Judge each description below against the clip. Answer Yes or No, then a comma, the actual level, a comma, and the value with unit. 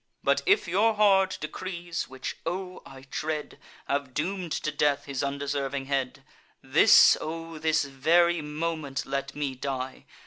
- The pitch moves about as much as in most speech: Yes, average, 3.8 semitones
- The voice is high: No, medium, 150 Hz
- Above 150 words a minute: No, slow, 135 wpm